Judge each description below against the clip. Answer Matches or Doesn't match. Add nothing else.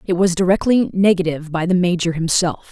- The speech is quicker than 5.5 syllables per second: Matches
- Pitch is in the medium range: Matches